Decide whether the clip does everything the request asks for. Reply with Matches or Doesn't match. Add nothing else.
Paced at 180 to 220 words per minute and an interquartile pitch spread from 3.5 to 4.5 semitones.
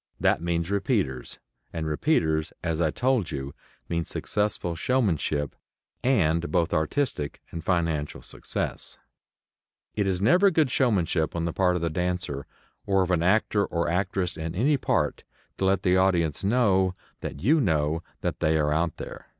Doesn't match